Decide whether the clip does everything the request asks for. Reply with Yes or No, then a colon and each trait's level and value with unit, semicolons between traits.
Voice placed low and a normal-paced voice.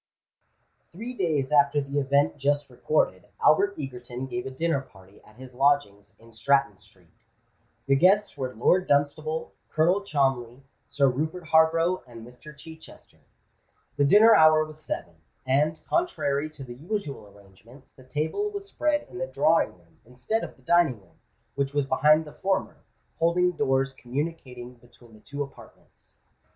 No: medium, 145 Hz; average, 155 wpm